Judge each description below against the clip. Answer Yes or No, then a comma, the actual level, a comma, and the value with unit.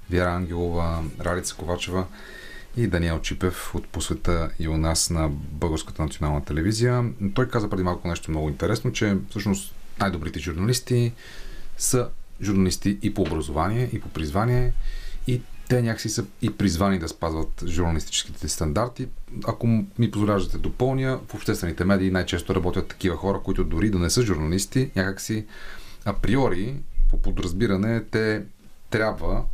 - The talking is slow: No, average, 140 wpm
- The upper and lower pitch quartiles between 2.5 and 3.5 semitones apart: No, average, 4.1 semitones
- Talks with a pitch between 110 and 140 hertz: No, very low, 95 Hz